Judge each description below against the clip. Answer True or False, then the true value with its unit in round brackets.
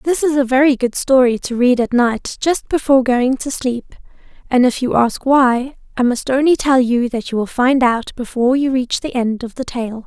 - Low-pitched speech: False (255 Hz)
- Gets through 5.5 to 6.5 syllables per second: False (4.9 syllables/s)